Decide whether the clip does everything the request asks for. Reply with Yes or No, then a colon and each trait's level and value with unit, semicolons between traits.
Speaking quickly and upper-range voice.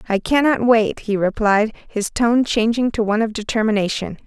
No: average, 170 wpm; high, 220 Hz